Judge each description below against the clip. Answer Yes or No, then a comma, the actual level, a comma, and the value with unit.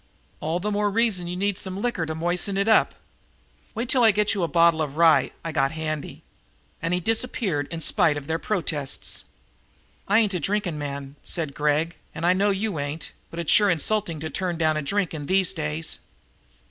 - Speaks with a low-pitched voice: No, medium, 170 Hz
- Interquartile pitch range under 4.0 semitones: No, average, 4.4 semitones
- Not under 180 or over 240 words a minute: Yes, average, 200 wpm